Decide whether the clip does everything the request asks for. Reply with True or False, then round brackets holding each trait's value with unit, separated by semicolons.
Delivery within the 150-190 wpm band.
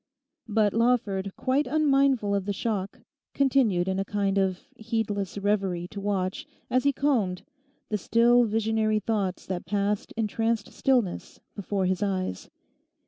False (140 wpm)